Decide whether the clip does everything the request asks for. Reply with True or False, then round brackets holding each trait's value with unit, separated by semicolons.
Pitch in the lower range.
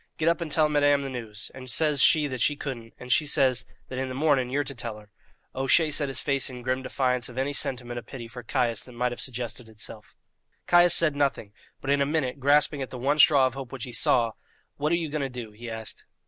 True (130 Hz)